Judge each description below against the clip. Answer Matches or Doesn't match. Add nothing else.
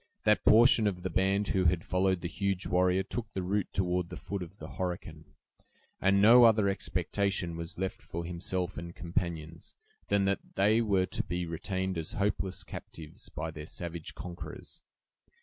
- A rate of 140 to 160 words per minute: Doesn't match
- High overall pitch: Doesn't match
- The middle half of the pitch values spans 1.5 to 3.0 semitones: Matches